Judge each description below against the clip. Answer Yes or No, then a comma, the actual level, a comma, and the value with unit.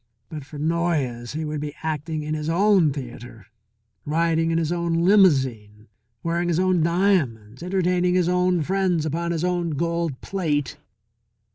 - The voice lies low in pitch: No, medium, 165 Hz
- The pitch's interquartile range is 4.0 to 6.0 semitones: No, average, 3.2 semitones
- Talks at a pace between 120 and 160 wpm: Yes, average, 150 wpm